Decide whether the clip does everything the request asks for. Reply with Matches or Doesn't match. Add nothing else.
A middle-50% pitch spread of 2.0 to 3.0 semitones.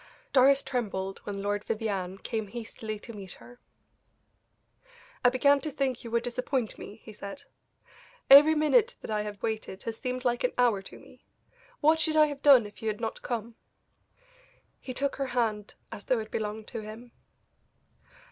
Doesn't match